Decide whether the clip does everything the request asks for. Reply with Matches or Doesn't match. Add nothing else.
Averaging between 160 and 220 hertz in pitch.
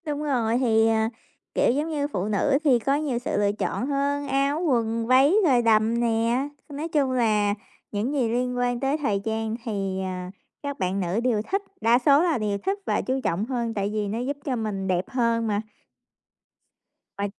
Doesn't match